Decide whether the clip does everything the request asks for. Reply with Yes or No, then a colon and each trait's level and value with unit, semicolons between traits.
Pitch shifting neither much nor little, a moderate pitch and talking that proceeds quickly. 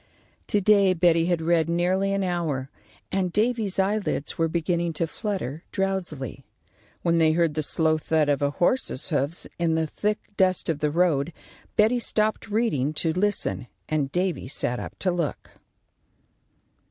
No: average, 3.7 semitones; medium, 170 Hz; average, 155 wpm